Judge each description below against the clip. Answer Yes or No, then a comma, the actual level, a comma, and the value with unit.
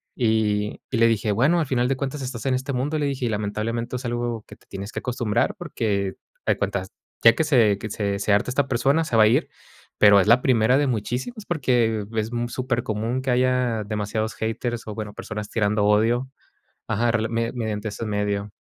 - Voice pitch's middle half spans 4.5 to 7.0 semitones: No, average, 3.1 semitones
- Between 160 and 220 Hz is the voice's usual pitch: No, low, 115 Hz